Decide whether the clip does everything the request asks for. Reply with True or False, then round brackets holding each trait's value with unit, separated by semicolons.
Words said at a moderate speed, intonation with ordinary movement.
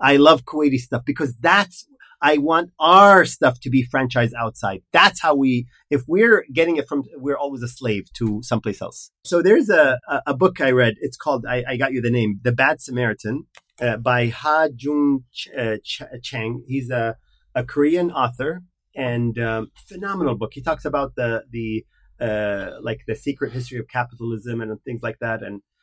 True (190 wpm; 3.8 semitones)